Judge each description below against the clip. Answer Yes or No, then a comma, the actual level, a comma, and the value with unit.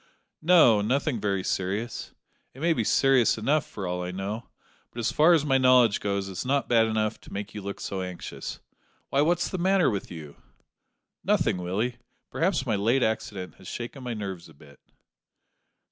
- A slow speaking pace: No, average, 180 wpm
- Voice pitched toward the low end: Yes, low, 110 Hz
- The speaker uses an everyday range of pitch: No, wide, 5.7 semitones